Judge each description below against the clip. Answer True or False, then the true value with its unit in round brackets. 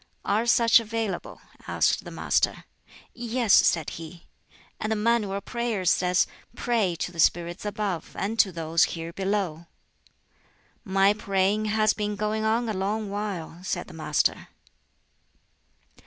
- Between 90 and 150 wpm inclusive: True (140 wpm)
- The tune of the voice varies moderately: True (3.5 semitones)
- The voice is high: True (200 Hz)